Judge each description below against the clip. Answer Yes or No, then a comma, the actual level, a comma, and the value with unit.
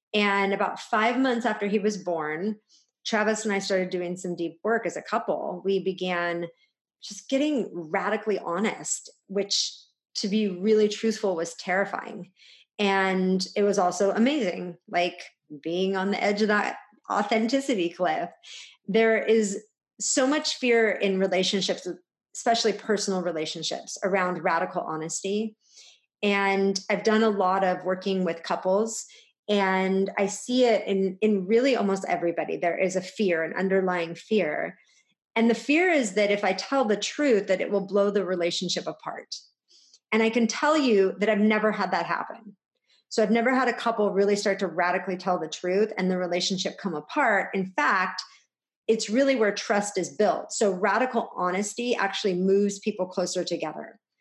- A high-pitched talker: Yes, high, 200 Hz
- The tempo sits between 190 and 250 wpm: No, average, 160 wpm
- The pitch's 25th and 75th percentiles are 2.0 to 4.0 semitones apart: Yes, average, 2.9 semitones